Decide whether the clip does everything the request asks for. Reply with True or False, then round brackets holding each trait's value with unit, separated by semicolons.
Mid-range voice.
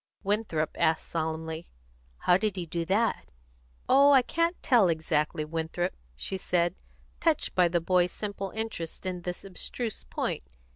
True (180 Hz)